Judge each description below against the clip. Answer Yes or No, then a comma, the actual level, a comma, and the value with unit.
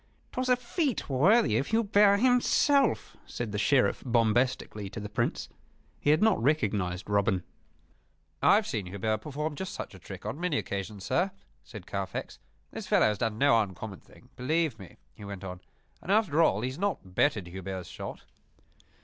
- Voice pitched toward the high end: No, low, 120 Hz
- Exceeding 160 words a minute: Yes, average, 175 wpm